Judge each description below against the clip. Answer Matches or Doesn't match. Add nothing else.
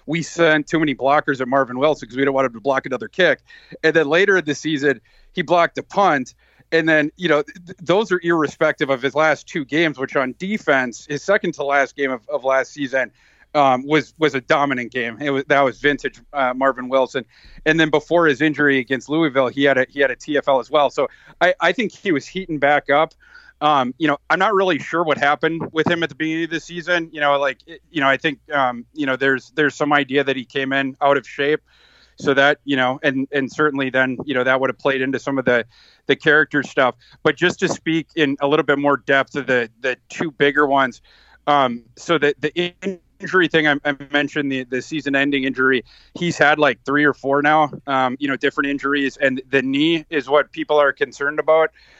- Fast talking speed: Matches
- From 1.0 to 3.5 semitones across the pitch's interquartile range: Matches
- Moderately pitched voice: Matches